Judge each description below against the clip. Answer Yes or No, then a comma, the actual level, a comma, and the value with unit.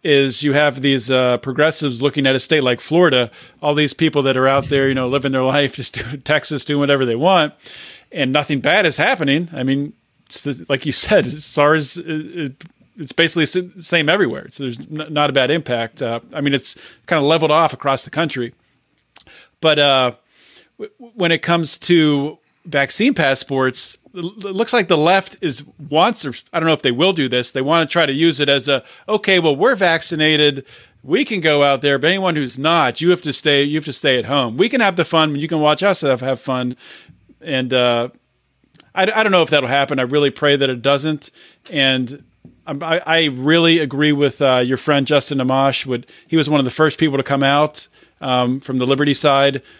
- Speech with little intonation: No, average, 3.2 semitones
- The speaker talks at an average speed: No, fast, 215 wpm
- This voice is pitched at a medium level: Yes, medium, 145 Hz